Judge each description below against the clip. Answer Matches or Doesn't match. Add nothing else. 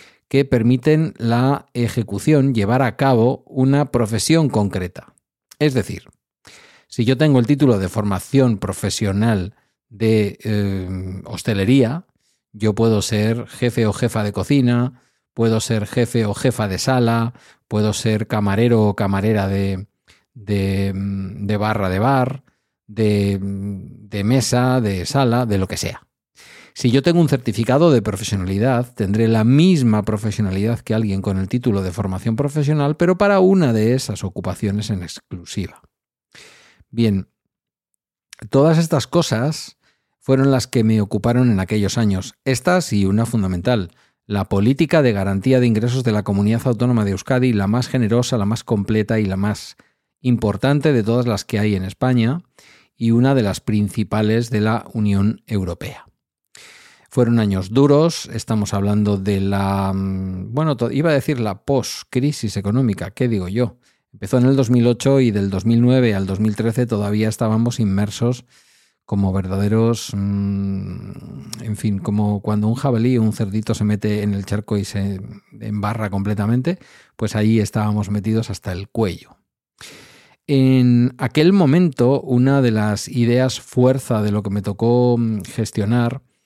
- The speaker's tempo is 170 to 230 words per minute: Doesn't match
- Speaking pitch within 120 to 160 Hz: Doesn't match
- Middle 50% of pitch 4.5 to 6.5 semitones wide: Doesn't match